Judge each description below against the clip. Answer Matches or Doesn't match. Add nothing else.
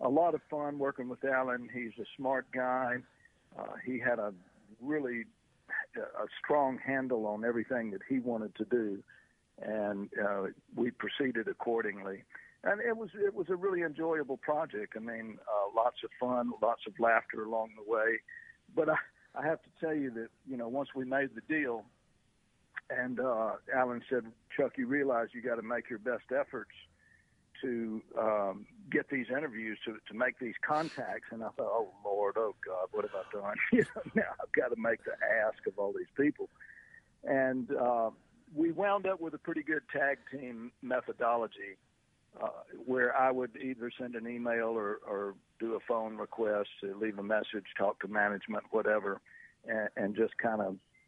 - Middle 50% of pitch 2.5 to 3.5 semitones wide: Doesn't match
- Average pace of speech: Matches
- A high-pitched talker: Doesn't match